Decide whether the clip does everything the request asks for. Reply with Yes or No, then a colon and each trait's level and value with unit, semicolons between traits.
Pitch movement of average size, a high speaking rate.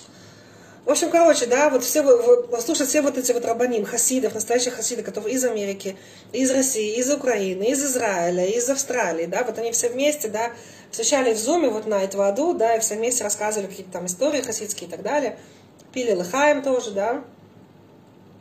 Yes: average, 4.5 semitones; fast, 185 wpm